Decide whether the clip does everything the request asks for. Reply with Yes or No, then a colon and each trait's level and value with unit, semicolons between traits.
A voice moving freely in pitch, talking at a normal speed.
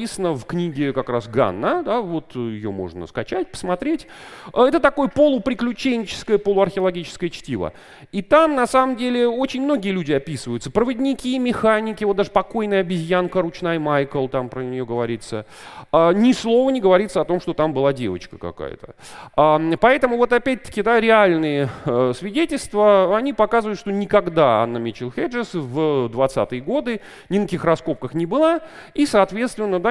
Yes: wide, 8.8 semitones; average, 145 wpm